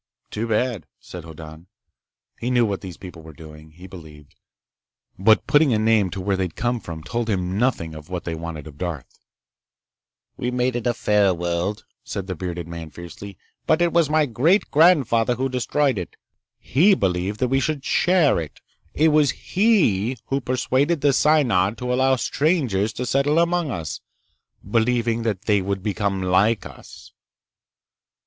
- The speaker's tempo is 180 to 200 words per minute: No, average, 170 wpm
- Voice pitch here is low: Yes, low, 110 Hz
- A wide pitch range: Yes, wide, 6.6 semitones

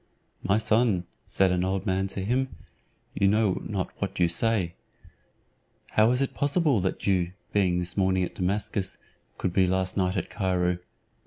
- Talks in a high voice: No, very low, 95 Hz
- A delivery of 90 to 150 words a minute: No, average, 165 wpm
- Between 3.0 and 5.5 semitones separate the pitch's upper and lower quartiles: No, narrow, 2.6 semitones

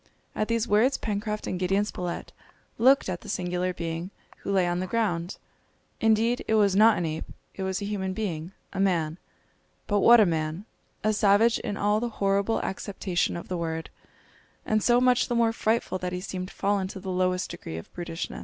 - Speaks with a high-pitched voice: Yes, high, 195 Hz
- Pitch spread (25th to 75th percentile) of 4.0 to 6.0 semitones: No, average, 3.2 semitones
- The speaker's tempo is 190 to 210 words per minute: Yes, average, 195 wpm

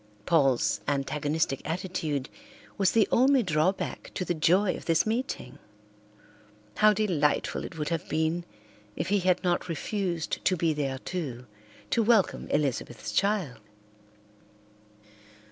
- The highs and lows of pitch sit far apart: No, average, 4.6 semitones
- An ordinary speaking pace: No, slow, 125 wpm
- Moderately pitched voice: Yes, medium, 170 Hz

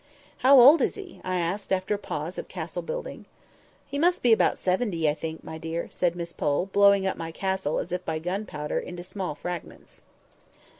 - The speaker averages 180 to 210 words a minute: Yes, average, 200 wpm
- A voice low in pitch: No, medium, 185 Hz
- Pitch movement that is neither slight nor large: Yes, average, 4.0 semitones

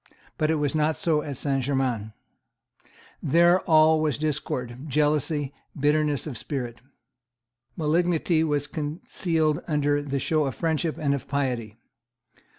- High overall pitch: No, medium, 150 Hz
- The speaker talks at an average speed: No, slow, 130 wpm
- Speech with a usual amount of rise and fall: No, narrow, 2.3 semitones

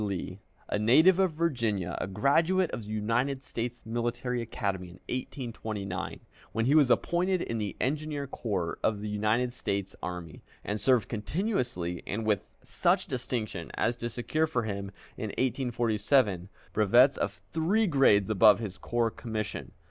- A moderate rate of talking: Yes, average, 150 wpm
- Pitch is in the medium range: No, low, 115 Hz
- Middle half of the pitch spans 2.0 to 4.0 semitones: No, average, 4.5 semitones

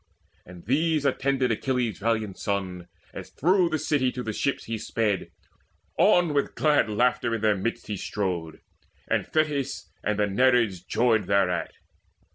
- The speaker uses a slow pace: No, average, 150 wpm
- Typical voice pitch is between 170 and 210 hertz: No, low, 115 Hz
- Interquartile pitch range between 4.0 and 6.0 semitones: Yes, average, 5.3 semitones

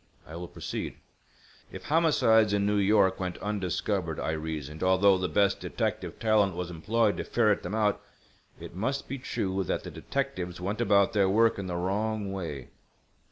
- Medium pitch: No, low, 100 Hz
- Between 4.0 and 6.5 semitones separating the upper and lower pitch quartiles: No, average, 3.1 semitones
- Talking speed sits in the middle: Yes, average, 170 wpm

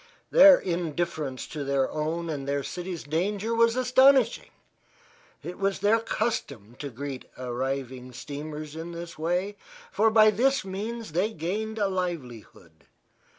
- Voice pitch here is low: No, medium, 175 Hz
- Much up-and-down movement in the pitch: Yes, wide, 7.1 semitones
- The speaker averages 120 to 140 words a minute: Yes, slow, 135 wpm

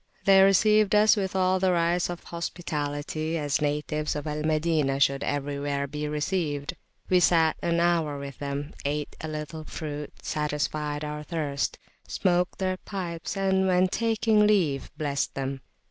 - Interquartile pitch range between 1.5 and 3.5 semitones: No, average, 3.9 semitones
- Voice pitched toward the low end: No, medium, 155 Hz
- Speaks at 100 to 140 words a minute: No, average, 150 wpm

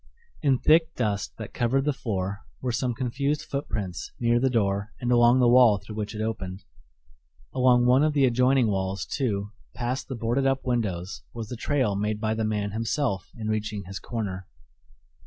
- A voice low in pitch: Yes, low, 115 Hz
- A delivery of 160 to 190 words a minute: Yes, average, 180 wpm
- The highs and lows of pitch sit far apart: No, average, 3.8 semitones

